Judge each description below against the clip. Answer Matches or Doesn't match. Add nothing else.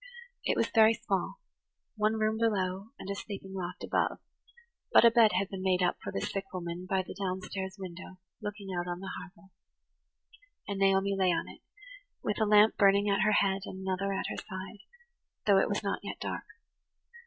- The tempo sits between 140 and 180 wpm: Doesn't match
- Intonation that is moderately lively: Doesn't match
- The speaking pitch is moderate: Doesn't match